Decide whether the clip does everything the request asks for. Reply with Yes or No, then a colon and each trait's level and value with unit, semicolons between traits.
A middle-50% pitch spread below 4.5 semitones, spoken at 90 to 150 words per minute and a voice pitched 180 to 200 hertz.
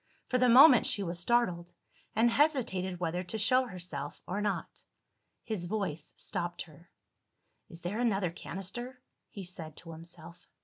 No: average, 5.2 semitones; average, 145 wpm; medium, 185 Hz